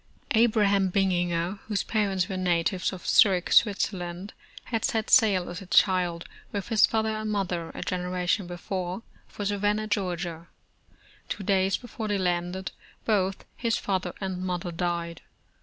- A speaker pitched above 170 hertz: Yes, high, 190 Hz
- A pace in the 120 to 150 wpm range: Yes, average, 145 wpm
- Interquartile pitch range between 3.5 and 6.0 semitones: No, average, 2.7 semitones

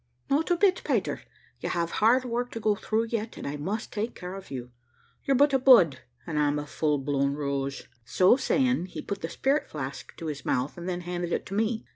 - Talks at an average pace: No, fast, 225 wpm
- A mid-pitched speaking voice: Yes, medium, 180 Hz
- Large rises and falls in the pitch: Yes, wide, 8.1 semitones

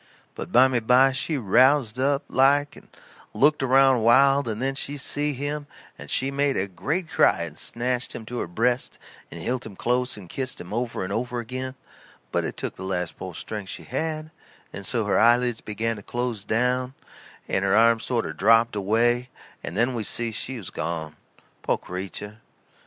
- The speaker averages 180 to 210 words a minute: Yes, average, 185 wpm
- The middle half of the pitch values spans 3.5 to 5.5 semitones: Yes, average, 3.9 semitones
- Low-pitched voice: Yes, low, 120 Hz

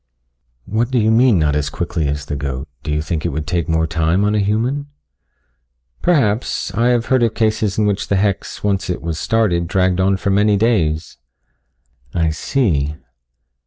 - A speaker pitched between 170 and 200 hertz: No, very low, 95 Hz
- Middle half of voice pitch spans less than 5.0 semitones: No, wide, 5.4 semitones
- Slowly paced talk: No, average, 185 wpm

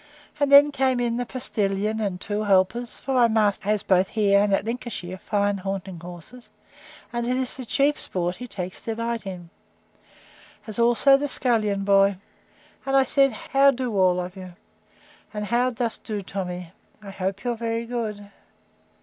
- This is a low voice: No, high, 215 Hz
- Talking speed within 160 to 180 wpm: Yes, average, 170 wpm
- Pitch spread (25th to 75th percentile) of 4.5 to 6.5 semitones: No, average, 3.9 semitones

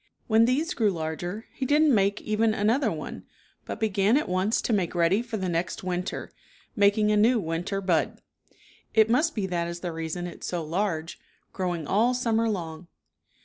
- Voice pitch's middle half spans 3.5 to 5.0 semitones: Yes, average, 4.3 semitones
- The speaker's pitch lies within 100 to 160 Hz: No, high, 200 Hz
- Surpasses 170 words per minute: Yes, average, 185 wpm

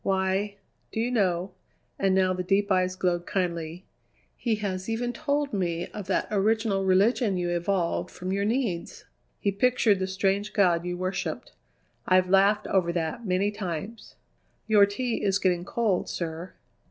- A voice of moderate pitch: No, high, 195 Hz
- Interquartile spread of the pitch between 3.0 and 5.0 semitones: No, narrow, 2.4 semitones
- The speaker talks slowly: No, average, 155 wpm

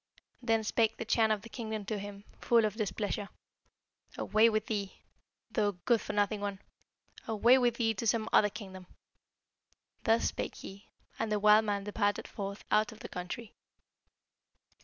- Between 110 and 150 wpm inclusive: No, average, 160 wpm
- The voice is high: Yes, high, 215 Hz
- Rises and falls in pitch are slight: Yes, narrow, 1.7 semitones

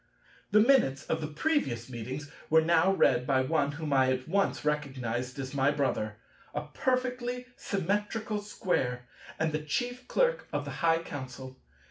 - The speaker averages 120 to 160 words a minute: Yes, average, 155 wpm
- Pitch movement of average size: No, wide, 7.9 semitones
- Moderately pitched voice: Yes, medium, 150 Hz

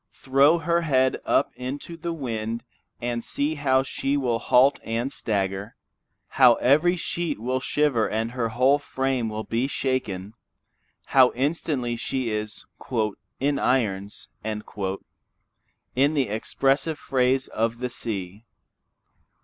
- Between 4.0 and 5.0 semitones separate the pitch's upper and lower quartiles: No, average, 3.6 semitones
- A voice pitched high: No, low, 125 Hz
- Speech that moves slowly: Yes, slow, 120 wpm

